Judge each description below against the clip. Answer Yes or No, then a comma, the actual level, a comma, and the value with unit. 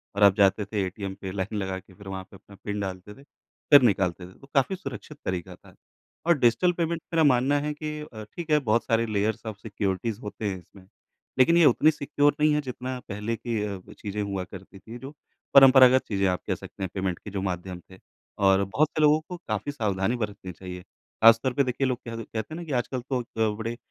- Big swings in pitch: Yes, wide, 5.7 semitones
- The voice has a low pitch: Yes, low, 110 Hz